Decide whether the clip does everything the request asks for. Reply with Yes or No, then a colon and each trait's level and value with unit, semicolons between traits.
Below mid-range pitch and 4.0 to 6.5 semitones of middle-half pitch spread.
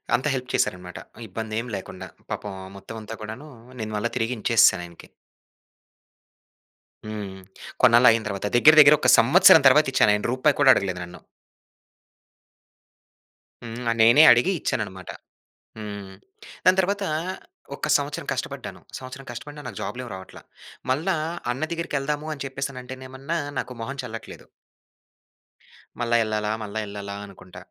Yes: low, 115 Hz; average, 4.5 semitones